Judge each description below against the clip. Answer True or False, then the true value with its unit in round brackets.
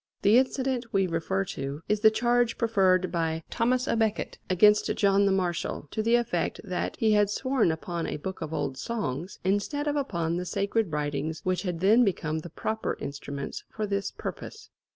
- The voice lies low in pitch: False (195 Hz)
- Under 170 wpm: False (185 wpm)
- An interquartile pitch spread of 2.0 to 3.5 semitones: False (5.2 semitones)